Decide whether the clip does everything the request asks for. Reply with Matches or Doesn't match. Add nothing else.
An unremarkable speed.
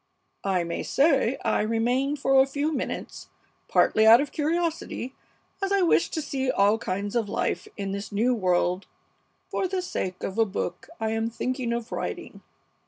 Matches